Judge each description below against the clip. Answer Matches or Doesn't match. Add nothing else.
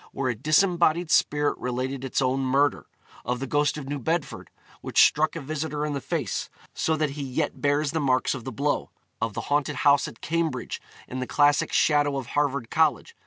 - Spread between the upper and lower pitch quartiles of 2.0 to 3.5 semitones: Matches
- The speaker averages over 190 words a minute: Matches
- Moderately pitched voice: Matches